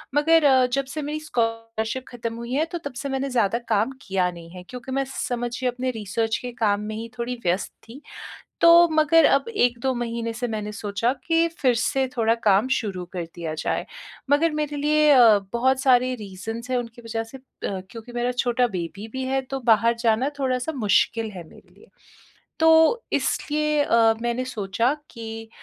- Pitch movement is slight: No, average, 3.2 semitones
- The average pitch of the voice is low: No, high, 240 Hz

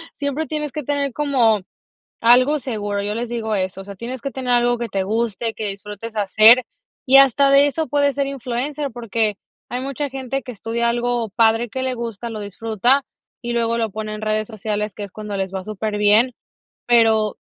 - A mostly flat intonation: No, average, 3.5 semitones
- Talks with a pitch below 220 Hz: No, high, 235 Hz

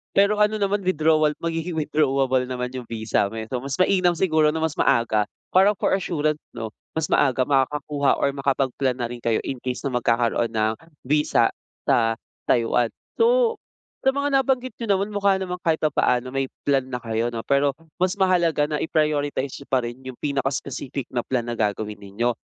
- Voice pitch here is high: No, medium, 140 Hz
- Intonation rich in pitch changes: Yes, wide, 6.0 semitones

